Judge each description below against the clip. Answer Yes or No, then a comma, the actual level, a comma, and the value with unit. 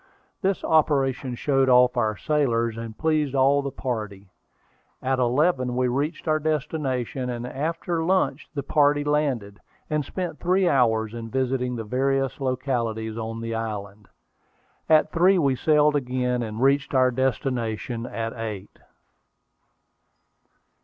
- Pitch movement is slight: No, average, 4.2 semitones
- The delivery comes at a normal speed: No, slow, 130 wpm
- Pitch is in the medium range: No, low, 130 Hz